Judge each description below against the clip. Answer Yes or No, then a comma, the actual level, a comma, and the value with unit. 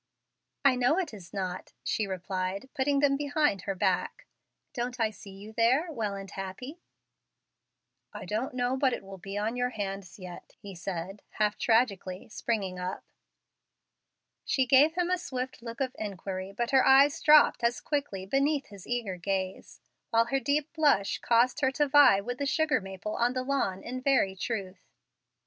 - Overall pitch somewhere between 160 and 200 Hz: No, high, 230 Hz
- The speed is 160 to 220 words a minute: Yes, average, 170 wpm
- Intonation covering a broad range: Yes, wide, 5.7 semitones